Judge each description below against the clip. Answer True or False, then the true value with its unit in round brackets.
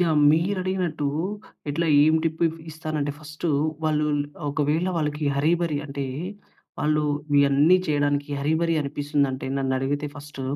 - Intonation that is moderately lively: False (1.9 semitones)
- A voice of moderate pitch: True (150 Hz)